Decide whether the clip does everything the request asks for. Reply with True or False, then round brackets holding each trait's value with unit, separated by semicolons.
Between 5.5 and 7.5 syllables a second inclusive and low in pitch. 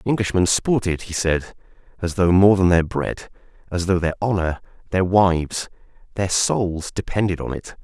False (4.8 syllables/s; 90 Hz)